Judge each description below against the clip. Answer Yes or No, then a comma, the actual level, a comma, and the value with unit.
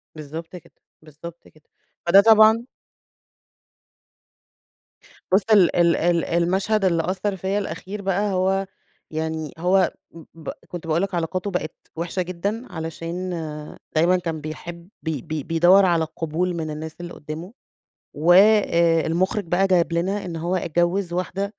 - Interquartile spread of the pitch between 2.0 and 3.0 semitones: Yes, average, 2.7 semitones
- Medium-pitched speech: Yes, medium, 175 Hz